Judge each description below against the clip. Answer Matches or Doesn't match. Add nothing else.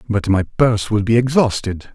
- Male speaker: Matches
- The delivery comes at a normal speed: Matches